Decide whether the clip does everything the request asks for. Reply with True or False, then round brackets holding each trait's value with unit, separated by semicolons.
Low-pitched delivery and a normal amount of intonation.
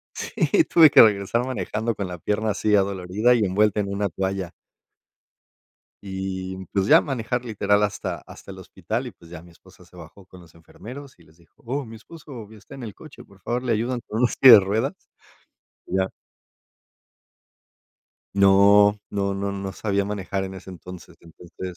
True (100 Hz; 3.0 semitones)